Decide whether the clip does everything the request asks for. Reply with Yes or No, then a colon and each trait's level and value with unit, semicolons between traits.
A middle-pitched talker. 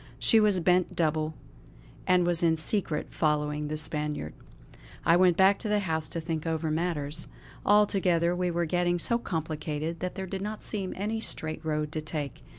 Yes: medium, 165 Hz